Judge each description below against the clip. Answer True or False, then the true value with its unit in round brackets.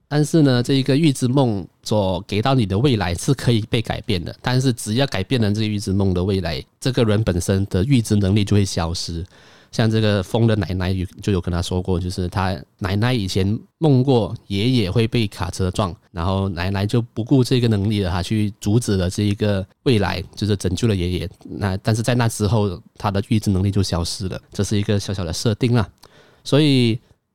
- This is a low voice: True (105 Hz)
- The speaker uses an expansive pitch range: False (3.8 semitones)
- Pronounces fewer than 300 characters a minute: False (310 characters per minute)